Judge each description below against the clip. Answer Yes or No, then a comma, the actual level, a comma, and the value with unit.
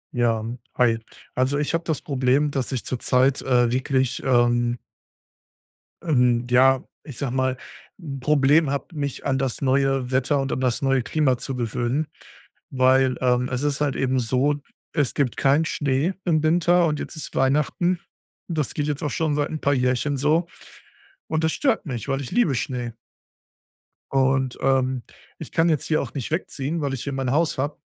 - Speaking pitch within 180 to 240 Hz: No, low, 135 Hz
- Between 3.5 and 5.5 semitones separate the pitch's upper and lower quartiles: No, average, 2.7 semitones